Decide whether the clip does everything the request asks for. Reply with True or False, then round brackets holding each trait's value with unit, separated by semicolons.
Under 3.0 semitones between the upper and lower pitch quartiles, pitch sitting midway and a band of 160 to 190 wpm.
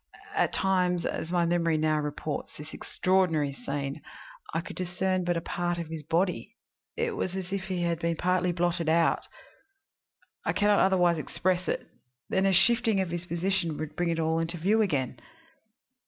True (2.5 semitones; 175 Hz; 180 wpm)